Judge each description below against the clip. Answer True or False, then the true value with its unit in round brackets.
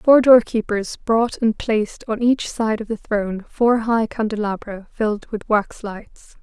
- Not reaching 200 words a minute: True (170 wpm)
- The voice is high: True (220 Hz)